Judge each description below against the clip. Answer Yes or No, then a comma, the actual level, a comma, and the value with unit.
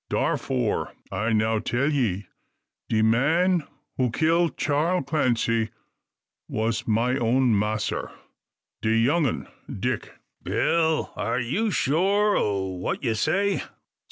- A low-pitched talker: Yes, low, 125 Hz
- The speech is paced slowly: Yes, slow, 115 wpm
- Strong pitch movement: Yes, wide, 6.3 semitones